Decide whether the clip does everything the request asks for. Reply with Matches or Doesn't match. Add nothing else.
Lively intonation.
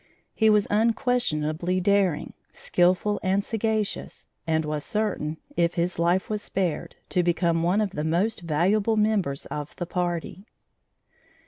Doesn't match